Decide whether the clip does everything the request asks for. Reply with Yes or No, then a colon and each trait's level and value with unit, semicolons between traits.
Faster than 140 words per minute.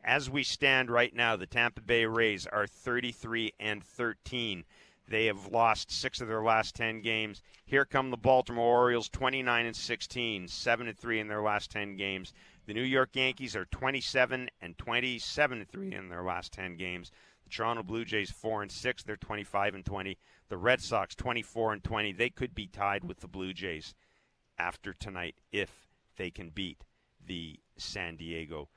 Yes: average, 175 wpm